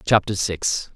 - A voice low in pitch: Yes, very low, 95 Hz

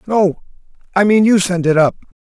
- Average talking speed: Yes, average, 190 wpm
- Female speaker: No, male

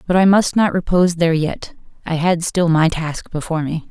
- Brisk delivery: Yes, fast, 215 wpm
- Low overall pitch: No, medium, 170 Hz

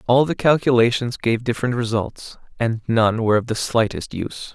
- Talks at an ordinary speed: Yes, average, 170 wpm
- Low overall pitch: Yes, low, 115 Hz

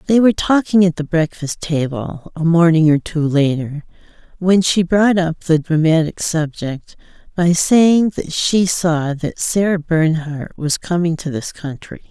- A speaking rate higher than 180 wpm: No, average, 160 wpm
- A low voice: No, medium, 165 Hz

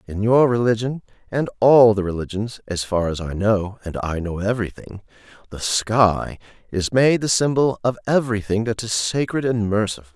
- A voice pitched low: Yes, low, 110 Hz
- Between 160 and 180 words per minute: Yes, average, 170 wpm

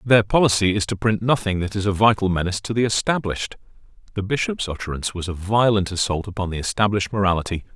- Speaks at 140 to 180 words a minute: No, average, 195 wpm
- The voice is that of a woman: No, male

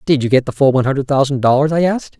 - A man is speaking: Yes, male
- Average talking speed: No, fast, 300 wpm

